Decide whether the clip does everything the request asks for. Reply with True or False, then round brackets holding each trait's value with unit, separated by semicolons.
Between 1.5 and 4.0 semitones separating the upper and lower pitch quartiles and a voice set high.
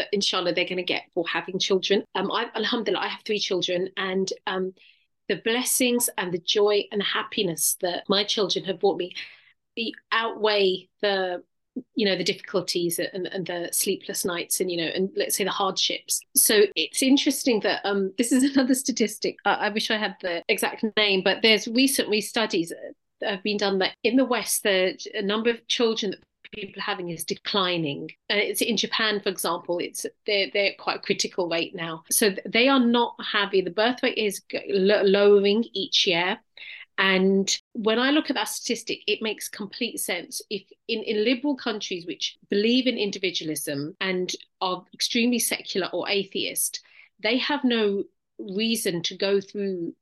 True (3.3 semitones; 205 Hz)